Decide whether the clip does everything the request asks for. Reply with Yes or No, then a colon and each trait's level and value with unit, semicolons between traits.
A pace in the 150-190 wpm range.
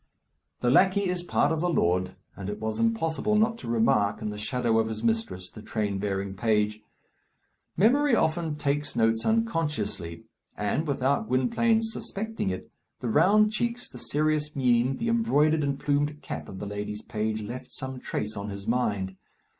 Yes: average, 170 wpm